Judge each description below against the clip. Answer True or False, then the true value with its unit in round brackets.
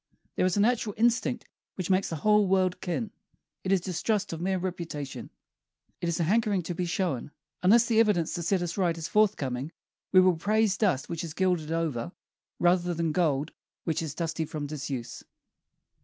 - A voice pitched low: False (175 Hz)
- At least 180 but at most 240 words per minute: True (185 wpm)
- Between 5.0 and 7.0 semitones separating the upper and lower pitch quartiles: False (3.6 semitones)